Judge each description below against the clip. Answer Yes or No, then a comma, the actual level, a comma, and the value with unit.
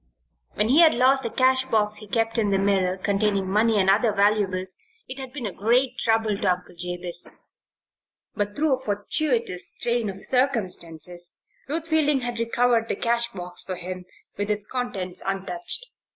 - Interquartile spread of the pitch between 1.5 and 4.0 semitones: No, average, 4.7 semitones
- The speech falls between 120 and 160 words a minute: No, average, 170 wpm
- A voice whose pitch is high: Yes, high, 210 Hz